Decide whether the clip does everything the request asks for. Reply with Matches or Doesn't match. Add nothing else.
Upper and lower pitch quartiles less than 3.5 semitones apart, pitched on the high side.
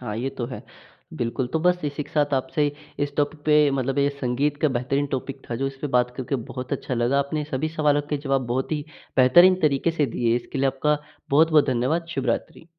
Doesn't match